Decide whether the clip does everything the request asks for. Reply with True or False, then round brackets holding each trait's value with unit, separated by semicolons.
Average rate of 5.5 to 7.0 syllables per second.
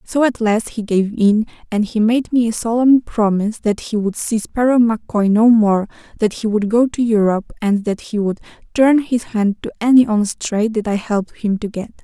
False (5.1 syllables/s)